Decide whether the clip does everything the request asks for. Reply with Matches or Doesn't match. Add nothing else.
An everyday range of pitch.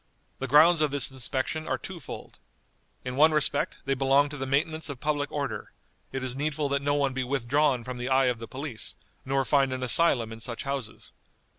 Doesn't match